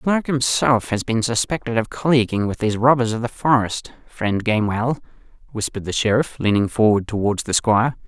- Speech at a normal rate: Yes, average, 180 wpm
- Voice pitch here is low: Yes, low, 115 Hz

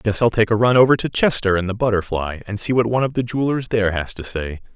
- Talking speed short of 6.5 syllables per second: No, 6.6 syllables/s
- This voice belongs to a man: Yes, male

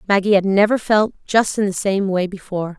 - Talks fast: Yes, fast, 215 wpm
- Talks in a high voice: Yes, high, 195 Hz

